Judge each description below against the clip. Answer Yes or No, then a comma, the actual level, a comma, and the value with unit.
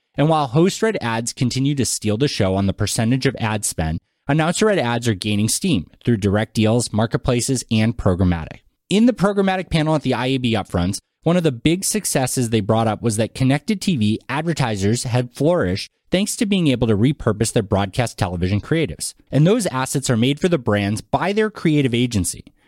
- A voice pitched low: Yes, low, 125 Hz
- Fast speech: No, average, 195 wpm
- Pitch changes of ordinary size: No, wide, 6.3 semitones